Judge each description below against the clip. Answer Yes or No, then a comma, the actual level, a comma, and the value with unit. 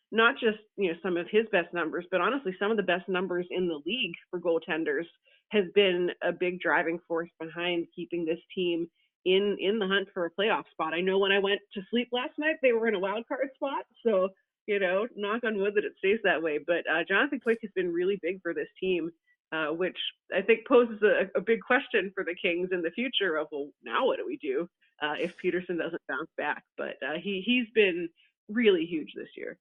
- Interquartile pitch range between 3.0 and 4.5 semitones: No, average, 5.1 semitones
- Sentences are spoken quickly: Yes, fast, 230 wpm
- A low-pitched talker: No, high, 195 Hz